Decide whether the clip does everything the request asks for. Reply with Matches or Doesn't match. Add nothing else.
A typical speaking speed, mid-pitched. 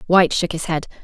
Doesn't match